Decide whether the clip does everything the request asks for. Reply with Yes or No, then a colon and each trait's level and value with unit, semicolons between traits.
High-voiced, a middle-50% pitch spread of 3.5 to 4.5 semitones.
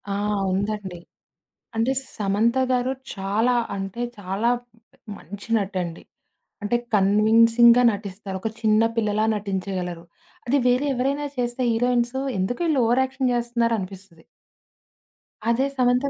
Yes: high, 225 Hz; average, 3.9 semitones